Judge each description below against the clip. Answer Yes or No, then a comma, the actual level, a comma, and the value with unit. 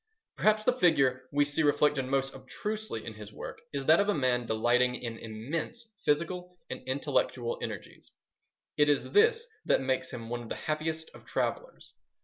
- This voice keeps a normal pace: Yes, average, 170 wpm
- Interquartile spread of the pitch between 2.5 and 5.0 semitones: No, wide, 5.6 semitones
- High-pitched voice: No, medium, 145 Hz